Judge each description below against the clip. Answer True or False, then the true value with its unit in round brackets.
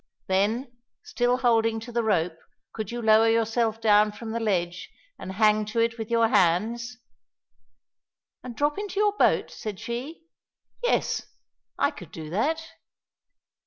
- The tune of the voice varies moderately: False (2.3 semitones)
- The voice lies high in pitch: True (225 Hz)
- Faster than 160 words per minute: False (145 wpm)